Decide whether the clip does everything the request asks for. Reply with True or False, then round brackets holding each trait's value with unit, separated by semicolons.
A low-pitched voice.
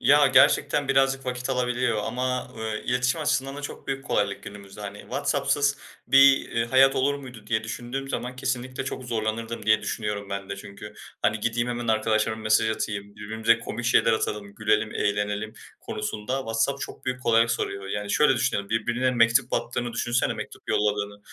True (115 Hz)